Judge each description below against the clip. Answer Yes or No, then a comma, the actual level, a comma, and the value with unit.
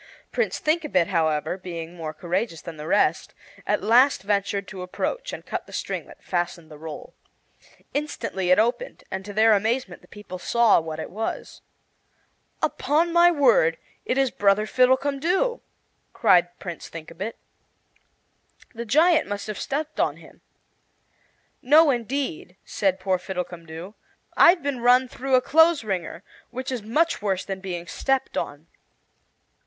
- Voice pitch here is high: Yes, high, 210 Hz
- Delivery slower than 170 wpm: Yes, average, 145 wpm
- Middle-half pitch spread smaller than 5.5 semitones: No, wide, 7.2 semitones